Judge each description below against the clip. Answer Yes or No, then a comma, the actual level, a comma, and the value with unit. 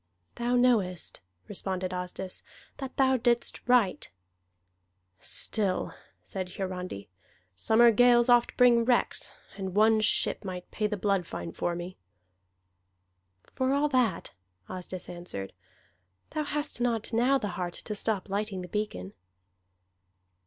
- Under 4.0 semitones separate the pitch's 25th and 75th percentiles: No, average, 4.9 semitones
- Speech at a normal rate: No, slow, 125 wpm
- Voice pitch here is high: Yes, high, 210 Hz